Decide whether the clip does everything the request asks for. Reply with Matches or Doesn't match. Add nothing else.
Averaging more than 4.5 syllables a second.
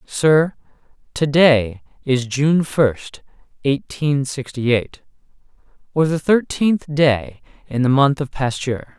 Doesn't match